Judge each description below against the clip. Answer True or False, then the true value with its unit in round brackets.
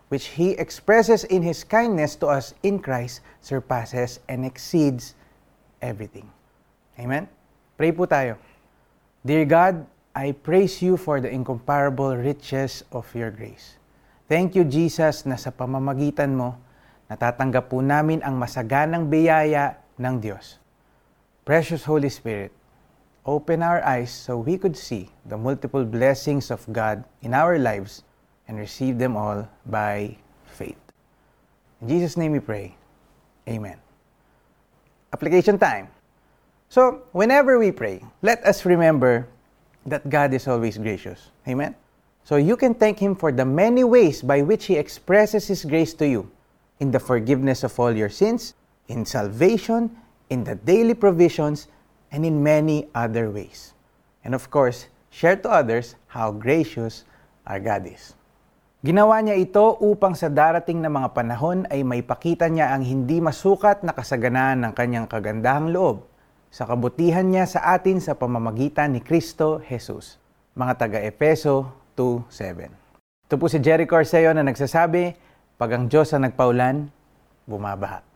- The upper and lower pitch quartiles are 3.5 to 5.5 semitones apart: True (5.2 semitones)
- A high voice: False (140 Hz)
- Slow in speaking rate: False (140 wpm)